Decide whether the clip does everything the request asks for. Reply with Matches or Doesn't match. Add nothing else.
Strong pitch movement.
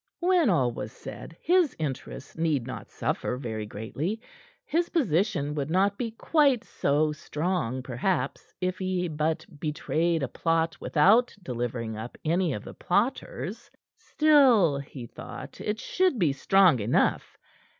Matches